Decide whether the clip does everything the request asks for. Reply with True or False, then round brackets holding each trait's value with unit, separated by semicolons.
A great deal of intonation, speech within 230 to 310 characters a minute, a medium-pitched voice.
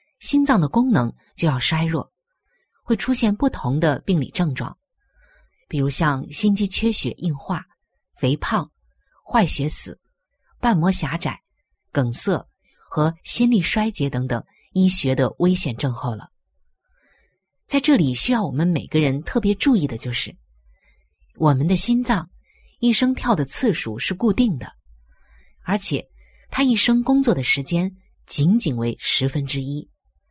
False (8.6 semitones; 205 characters per minute; 160 Hz)